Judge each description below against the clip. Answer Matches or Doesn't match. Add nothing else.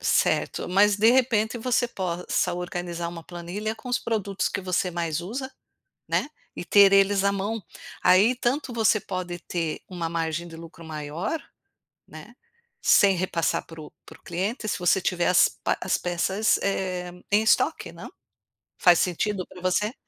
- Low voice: Doesn't match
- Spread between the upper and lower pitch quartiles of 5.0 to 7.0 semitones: Doesn't match